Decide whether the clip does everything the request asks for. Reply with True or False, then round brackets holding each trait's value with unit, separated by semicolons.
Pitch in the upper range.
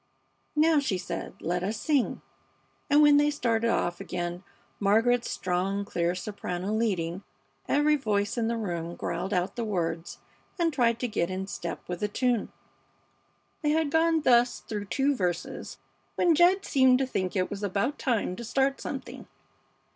True (220 Hz)